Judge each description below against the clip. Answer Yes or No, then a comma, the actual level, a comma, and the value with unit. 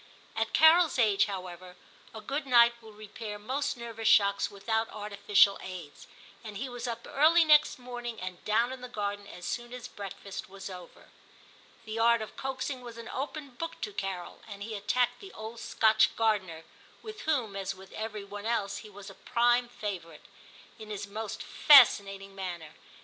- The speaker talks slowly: No, average, 180 wpm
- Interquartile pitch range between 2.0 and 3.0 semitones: No, average, 3.5 semitones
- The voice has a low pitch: No, high, 220 Hz